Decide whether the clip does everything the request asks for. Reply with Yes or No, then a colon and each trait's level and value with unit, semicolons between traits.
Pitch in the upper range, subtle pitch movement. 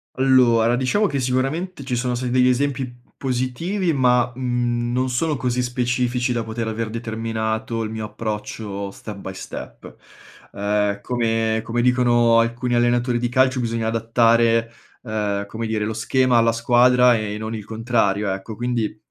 No: low, 120 Hz; narrow, 2.1 semitones